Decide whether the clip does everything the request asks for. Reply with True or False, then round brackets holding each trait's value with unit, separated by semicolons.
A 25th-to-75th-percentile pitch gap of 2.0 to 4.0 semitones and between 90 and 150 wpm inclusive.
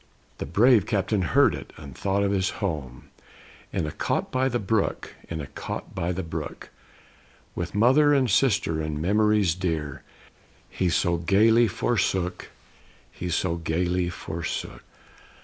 False (4.4 semitones; 145 wpm)